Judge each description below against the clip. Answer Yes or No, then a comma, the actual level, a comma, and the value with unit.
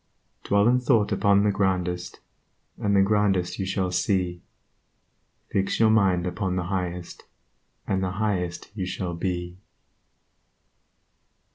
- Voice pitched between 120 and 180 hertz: No, very low, 95 Hz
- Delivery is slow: Yes, slow, 125 wpm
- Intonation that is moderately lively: No, narrow, 2.2 semitones